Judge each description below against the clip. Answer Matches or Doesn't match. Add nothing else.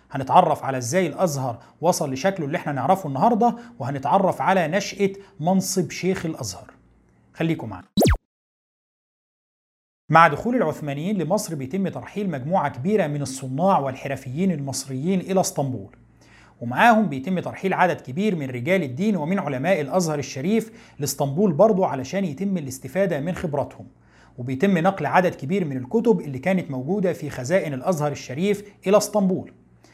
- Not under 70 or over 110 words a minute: Doesn't match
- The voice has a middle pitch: Matches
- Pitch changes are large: Matches